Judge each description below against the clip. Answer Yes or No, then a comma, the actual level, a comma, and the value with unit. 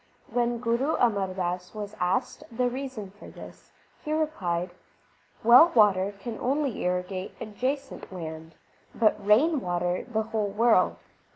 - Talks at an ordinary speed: No, slow, 130 wpm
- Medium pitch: No, high, 215 Hz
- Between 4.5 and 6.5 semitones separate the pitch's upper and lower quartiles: Yes, average, 5.1 semitones